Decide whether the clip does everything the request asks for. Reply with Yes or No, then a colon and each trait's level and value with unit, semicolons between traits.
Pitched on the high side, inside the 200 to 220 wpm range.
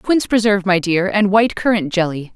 Yes: high, 200 Hz; fast, 205 wpm